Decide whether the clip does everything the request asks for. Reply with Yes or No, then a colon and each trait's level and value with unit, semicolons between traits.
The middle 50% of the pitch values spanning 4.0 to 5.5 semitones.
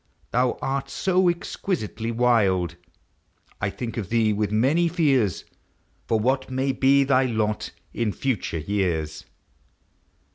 Yes: average, 4.6 semitones